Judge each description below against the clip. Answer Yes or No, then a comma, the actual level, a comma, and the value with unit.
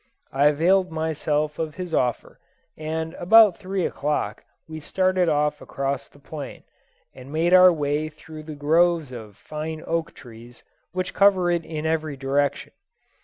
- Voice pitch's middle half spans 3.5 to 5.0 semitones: No, average, 3.1 semitones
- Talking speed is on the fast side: No, average, 150 wpm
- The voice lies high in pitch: No, medium, 155 Hz